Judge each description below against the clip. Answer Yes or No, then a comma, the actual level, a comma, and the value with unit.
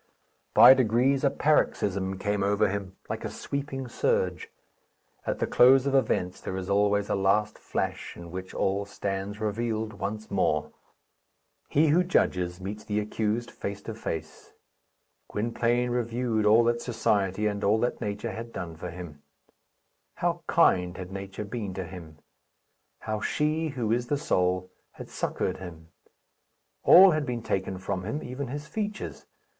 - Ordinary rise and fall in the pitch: Yes, average, 4.4 semitones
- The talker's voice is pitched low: Yes, low, 105 Hz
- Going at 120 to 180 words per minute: Yes, average, 155 wpm